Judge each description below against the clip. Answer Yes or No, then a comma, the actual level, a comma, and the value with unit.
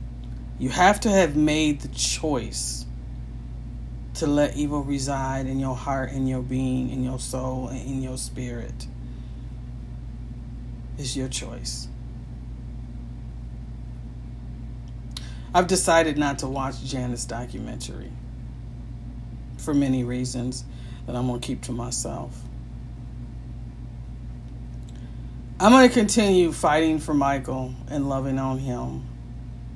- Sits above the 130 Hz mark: No, low, 125 Hz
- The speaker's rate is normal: No, slow, 110 wpm